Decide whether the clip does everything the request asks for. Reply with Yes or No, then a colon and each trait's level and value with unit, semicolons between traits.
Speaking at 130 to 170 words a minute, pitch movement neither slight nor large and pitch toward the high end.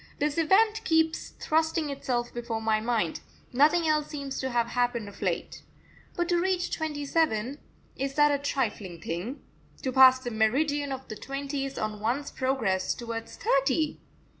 Yes: average, 160 wpm; average, 4.4 semitones; very high, 270 Hz